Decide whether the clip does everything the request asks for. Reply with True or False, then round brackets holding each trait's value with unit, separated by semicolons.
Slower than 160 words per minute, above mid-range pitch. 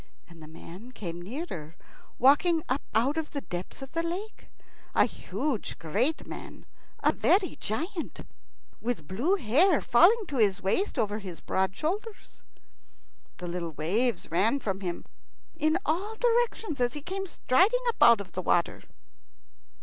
True (150 wpm; 255 Hz)